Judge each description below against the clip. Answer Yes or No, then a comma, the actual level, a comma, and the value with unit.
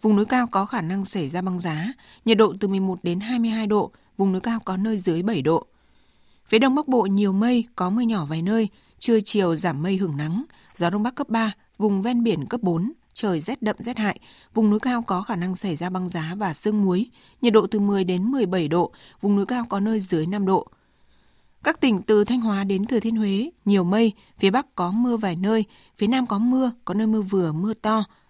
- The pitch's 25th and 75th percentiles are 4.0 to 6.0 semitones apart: No, average, 3.4 semitones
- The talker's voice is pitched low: No, high, 205 Hz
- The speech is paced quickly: No, average, 240 wpm